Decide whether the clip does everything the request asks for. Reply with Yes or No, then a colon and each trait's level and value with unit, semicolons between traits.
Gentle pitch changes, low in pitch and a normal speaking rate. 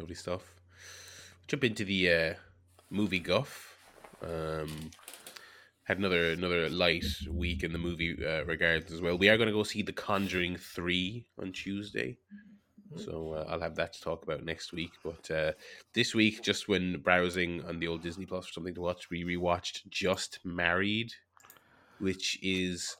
Yes: narrow, 2.3 semitones; very low, 90 Hz; average, 165 wpm